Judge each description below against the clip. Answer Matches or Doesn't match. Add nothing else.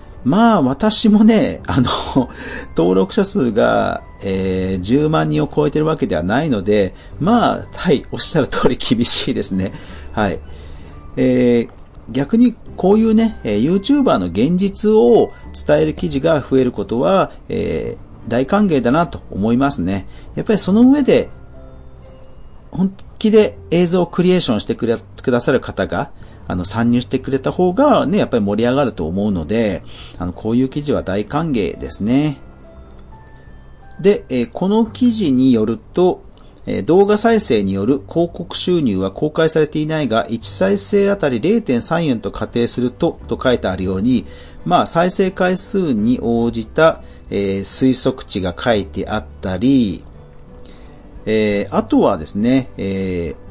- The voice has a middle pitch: Doesn't match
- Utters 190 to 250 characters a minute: Doesn't match